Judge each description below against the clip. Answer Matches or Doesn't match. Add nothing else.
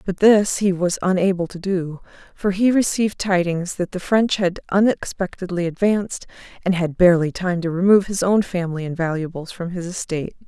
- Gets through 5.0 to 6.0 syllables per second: Matches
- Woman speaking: Matches